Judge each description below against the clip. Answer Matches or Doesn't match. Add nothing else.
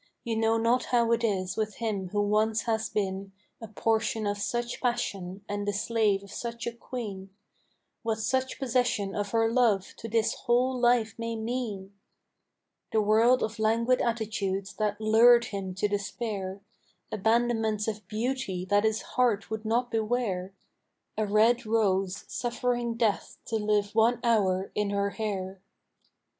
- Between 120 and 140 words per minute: Doesn't match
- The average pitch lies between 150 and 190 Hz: Doesn't match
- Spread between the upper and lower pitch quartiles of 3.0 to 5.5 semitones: Doesn't match